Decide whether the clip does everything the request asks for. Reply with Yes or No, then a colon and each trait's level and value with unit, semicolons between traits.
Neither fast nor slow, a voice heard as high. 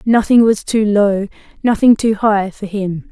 Yes: average, 175 wpm; high, 210 Hz